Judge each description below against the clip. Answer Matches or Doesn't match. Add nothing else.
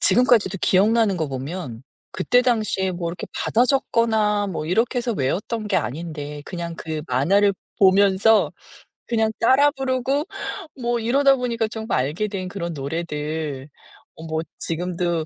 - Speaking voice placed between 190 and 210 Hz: Matches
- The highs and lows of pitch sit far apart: Matches